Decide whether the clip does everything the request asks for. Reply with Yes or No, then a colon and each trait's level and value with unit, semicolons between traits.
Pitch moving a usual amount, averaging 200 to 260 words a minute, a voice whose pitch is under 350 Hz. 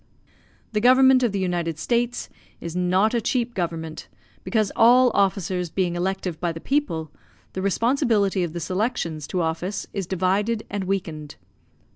No: average, 4.8 semitones; average, 150 wpm; high, 190 Hz